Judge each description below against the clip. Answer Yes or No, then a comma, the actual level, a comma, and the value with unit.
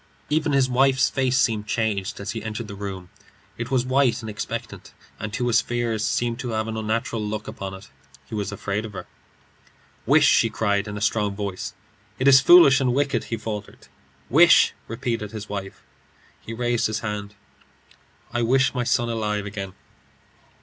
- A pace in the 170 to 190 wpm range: Yes, average, 175 wpm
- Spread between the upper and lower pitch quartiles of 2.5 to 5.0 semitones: Yes, average, 2.9 semitones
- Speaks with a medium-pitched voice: No, low, 110 Hz